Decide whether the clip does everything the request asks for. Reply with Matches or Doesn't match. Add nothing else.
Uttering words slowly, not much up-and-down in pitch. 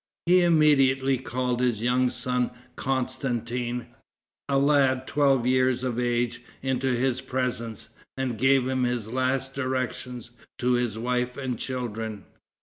Matches